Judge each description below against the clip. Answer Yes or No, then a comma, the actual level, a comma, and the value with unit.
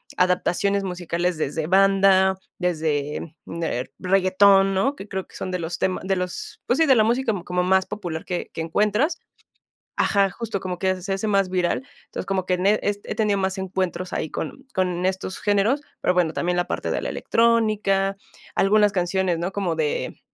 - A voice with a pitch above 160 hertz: Yes, high, 190 Hz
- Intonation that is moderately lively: No, narrow, 2.0 semitones